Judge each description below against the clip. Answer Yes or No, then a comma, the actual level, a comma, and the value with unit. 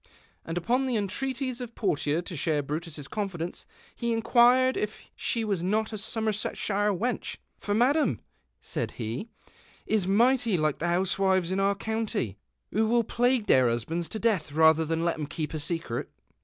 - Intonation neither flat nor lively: No, wide, 5.8 semitones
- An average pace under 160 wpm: No, average, 175 wpm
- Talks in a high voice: Yes, high, 195 Hz